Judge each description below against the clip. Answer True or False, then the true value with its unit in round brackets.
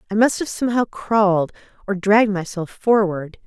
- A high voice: True (205 Hz)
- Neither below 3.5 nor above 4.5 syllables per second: False (5.4 syllables/s)